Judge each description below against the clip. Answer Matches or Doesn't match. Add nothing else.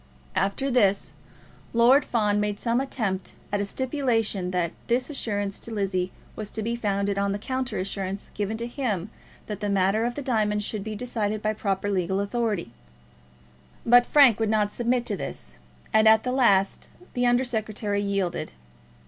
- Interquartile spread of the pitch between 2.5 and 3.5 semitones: Matches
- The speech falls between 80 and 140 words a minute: Doesn't match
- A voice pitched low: Doesn't match